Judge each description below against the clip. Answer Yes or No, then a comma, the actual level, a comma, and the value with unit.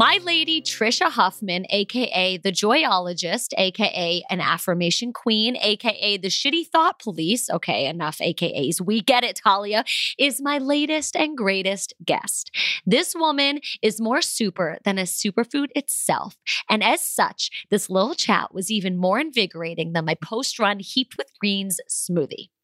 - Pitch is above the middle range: Yes, high, 210 Hz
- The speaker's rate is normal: Yes, average, 150 wpm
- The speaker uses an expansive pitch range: Yes, wide, 6.1 semitones